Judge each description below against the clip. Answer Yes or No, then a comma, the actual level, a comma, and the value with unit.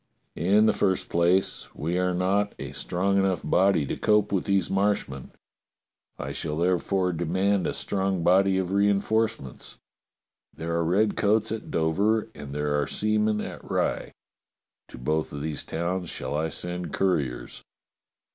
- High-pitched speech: No, very low, 95 Hz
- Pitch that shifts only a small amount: No, average, 3.6 semitones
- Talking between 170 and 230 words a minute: No, average, 145 wpm